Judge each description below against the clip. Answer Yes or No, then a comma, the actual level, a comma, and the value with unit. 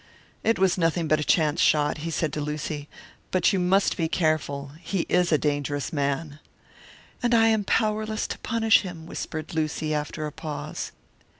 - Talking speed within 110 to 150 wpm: No, average, 175 wpm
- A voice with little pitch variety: No, average, 3.9 semitones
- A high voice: No, medium, 160 Hz